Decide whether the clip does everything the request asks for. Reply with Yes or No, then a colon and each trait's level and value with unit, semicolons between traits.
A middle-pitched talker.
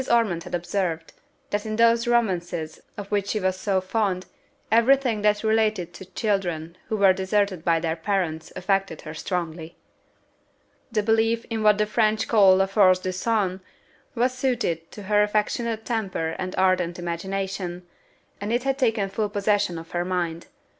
No: high, 195 Hz